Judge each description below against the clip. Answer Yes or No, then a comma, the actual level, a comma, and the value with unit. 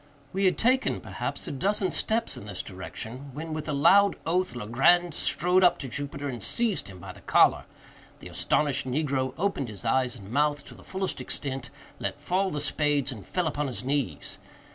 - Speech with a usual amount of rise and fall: No, wide, 5.8 semitones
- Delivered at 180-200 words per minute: Yes, average, 190 wpm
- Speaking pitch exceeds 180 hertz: No, medium, 145 Hz